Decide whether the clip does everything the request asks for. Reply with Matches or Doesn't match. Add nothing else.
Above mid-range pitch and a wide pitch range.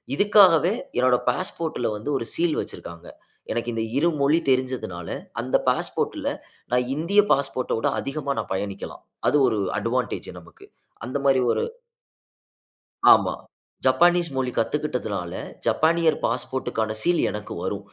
Doesn't match